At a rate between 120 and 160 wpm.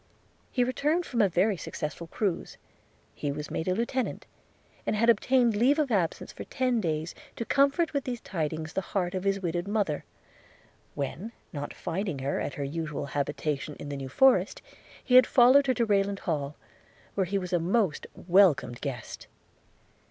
No: average, 175 wpm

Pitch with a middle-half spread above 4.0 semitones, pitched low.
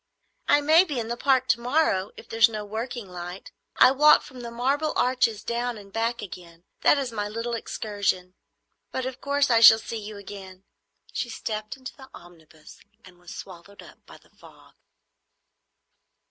No: average, 4.5 semitones; high, 225 Hz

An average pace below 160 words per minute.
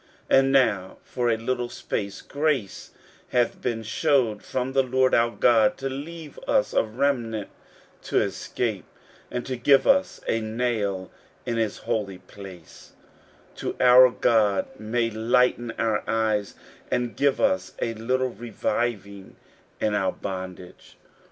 Yes: average, 140 wpm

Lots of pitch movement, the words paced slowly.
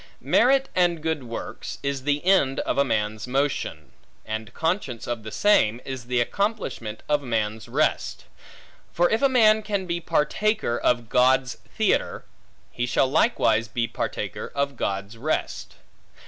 No: wide, 7.3 semitones; average, 145 wpm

